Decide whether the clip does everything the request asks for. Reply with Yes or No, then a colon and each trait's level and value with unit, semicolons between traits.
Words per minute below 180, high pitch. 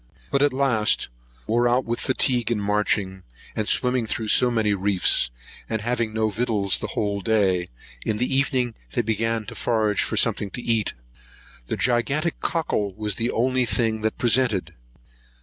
No: average, 165 wpm; low, 115 Hz